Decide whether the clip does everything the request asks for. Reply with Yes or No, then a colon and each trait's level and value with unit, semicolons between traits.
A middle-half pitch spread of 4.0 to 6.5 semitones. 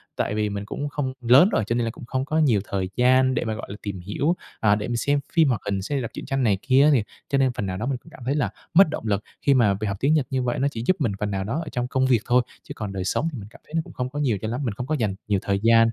Yes: average, 4.8 semitones